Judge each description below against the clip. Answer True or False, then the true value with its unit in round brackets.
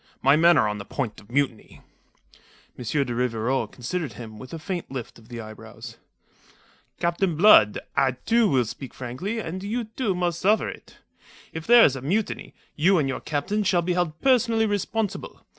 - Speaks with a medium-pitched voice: True (160 Hz)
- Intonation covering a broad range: True (8.0 semitones)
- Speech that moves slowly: False (180 wpm)